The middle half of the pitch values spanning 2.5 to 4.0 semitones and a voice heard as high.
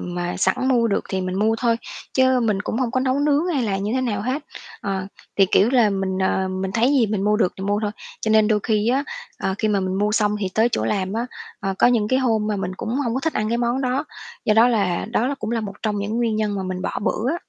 Yes: average, 3.7 semitones; high, 215 Hz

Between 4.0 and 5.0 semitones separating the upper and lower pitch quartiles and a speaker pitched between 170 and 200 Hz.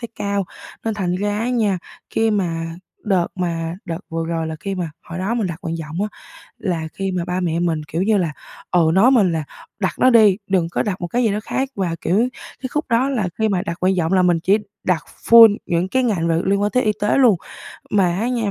Yes: average, 4.3 semitones; high, 190 Hz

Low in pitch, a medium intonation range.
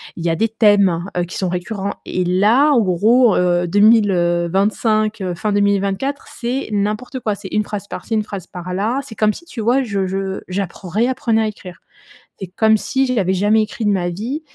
No: high, 205 Hz; average, 3.2 semitones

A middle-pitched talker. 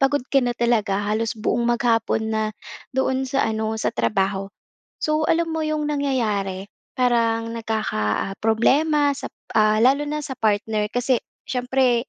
No: high, 235 Hz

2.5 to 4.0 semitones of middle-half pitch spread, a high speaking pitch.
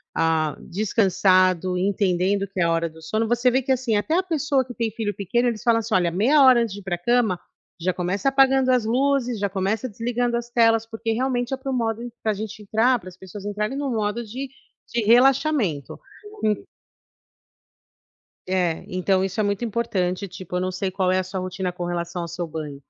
No: average, 4.6 semitones; high, 210 Hz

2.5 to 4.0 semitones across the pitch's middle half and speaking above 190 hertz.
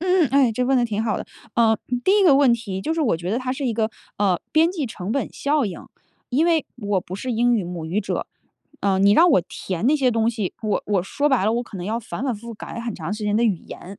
No: average, 4.8 semitones; high, 230 Hz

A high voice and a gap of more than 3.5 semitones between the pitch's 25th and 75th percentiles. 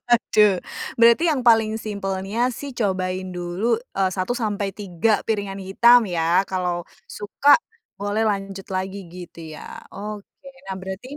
No: high, 200 Hz; average, 3.1 semitones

